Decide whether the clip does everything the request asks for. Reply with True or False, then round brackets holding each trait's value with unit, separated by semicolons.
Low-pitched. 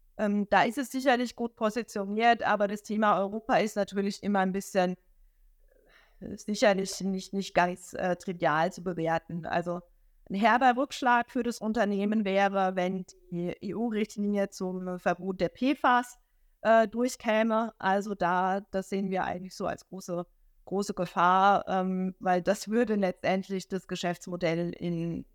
False (195 Hz)